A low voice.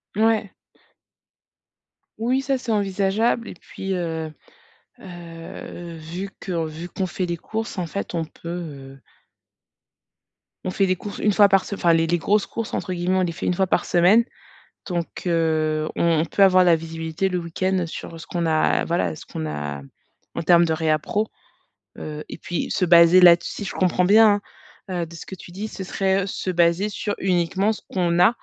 No: medium, 175 Hz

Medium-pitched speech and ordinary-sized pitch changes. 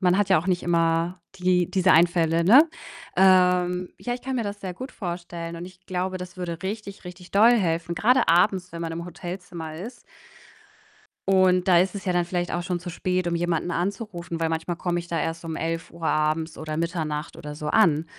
No: medium, 175 Hz; narrow, 1.9 semitones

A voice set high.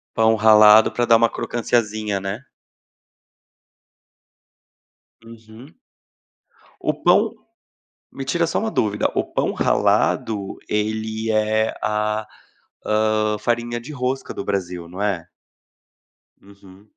No: low, 110 Hz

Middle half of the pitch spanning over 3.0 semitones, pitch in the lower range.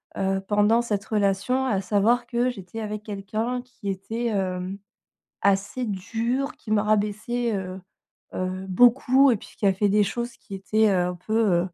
No: average, 3.5 semitones; high, 210 Hz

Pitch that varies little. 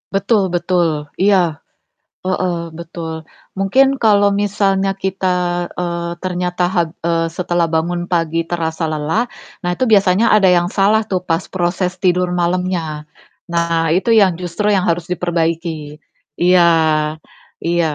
Yes: narrow, 2.2 semitones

